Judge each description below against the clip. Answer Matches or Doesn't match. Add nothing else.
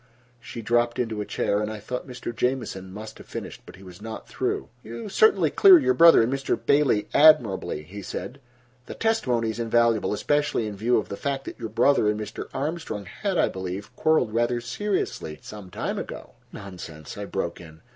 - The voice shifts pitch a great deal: Doesn't match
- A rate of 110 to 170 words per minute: Doesn't match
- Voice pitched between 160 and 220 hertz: Doesn't match